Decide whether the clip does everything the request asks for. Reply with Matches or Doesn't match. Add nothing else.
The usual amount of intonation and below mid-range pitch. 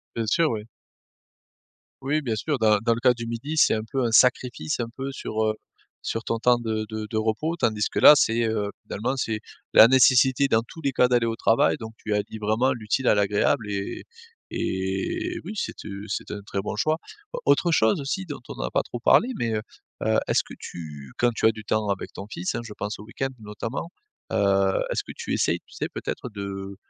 Matches